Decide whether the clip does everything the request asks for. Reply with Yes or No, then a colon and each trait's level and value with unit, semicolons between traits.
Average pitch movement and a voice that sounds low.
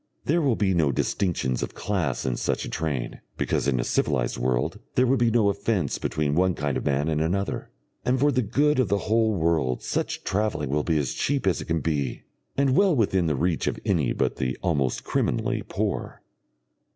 No: wide, 7.5 semitones; very low, 85 Hz